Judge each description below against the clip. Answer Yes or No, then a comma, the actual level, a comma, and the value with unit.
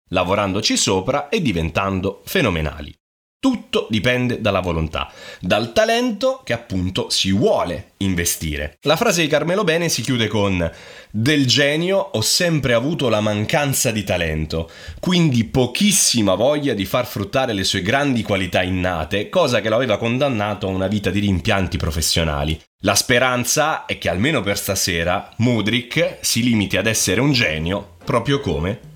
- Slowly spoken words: No, average, 145 wpm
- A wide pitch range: Yes, wide, 6.1 semitones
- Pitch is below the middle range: Yes, low, 105 Hz